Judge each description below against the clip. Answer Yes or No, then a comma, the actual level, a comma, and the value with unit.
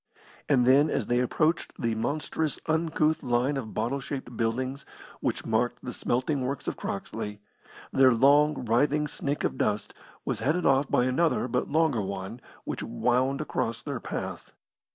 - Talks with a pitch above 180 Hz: No, low, 130 Hz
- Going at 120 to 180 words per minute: Yes, average, 155 wpm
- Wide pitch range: No, average, 3.7 semitones